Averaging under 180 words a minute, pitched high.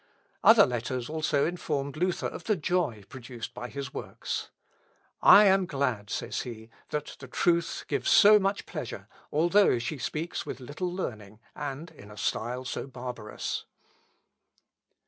No: average, 145 wpm; medium, 140 Hz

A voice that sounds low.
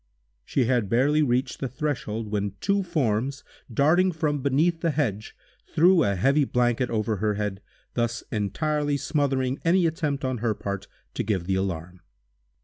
Yes: low, 130 Hz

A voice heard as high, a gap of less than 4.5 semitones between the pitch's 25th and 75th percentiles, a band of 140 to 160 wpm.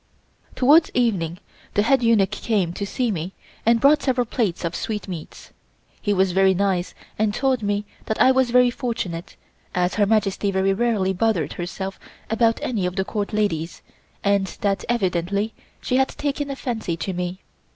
No: high, 205 Hz; average, 4.0 semitones; average, 170 wpm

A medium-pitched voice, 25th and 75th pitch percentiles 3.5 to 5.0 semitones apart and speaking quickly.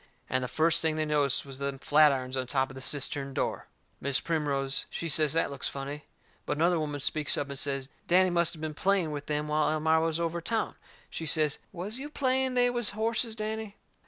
Yes: medium, 155 Hz; average, 4.0 semitones; fast, 215 wpm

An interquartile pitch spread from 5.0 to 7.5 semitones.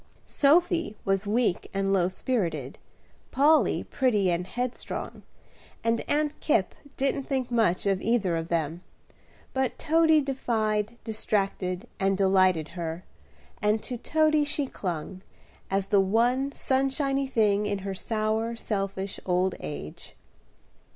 Yes: wide, 5.6 semitones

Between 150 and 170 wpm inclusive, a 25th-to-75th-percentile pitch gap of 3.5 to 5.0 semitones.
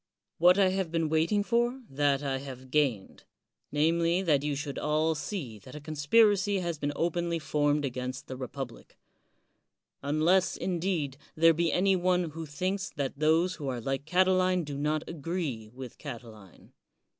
Yes: average, 160 wpm; average, 4.4 semitones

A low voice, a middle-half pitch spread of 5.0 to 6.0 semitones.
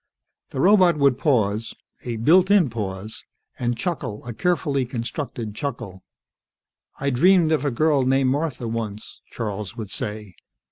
Yes: low, 125 Hz; wide, 5.4 semitones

